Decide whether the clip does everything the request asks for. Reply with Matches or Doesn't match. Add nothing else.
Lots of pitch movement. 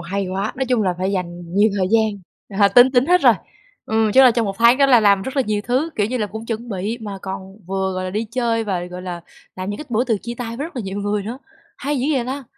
Doesn't match